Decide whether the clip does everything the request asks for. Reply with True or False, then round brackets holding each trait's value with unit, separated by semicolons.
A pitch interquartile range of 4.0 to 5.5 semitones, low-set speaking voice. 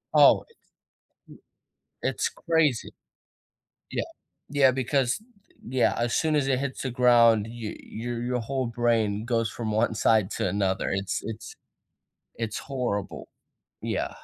False (3.0 semitones; 120 Hz)